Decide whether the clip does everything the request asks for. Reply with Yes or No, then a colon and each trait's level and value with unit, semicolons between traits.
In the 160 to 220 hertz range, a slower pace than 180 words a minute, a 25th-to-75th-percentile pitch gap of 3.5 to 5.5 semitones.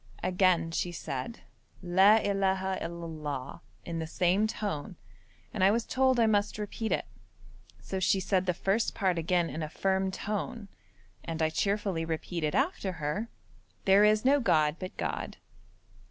Yes: high, 190 Hz; average, 155 wpm; average, 3.9 semitones